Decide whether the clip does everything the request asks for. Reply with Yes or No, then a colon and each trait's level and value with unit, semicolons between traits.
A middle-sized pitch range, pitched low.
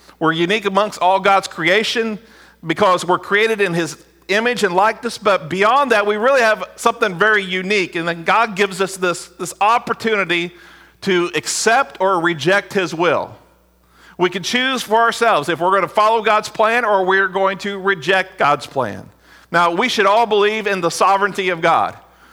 No: average, 3.7 semitones; high, 195 Hz